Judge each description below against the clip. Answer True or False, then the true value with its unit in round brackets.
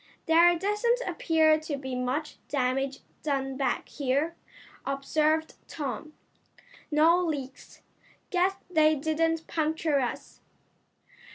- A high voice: True (310 Hz)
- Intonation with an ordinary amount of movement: True (3.0 semitones)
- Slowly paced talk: True (100 wpm)